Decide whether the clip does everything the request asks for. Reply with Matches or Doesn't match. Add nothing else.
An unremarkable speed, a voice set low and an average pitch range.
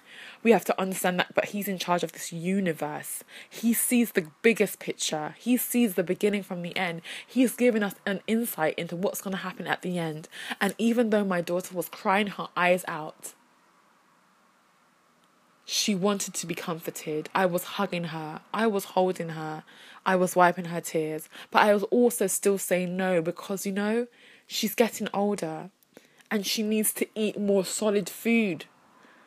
Doesn't match